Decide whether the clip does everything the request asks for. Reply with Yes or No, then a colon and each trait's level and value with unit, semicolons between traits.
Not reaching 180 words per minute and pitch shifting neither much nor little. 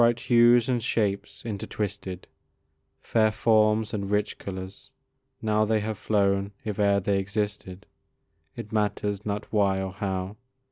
No: slow, 135 wpm; narrow, 1.7 semitones